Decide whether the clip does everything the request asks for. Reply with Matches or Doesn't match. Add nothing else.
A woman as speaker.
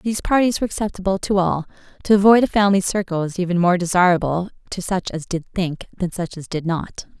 Matches